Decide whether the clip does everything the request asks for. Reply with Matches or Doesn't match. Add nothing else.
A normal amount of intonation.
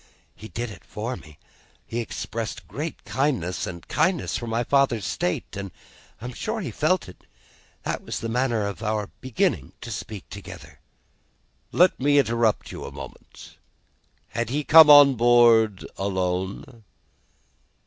Matches